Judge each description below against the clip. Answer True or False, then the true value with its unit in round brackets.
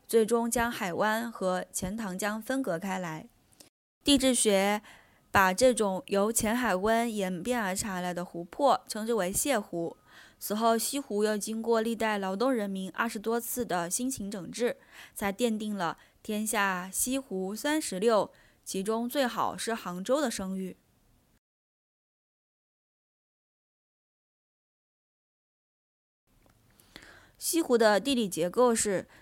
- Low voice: False (215 Hz)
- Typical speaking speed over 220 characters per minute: False (180 characters per minute)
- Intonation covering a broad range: False (3.7 semitones)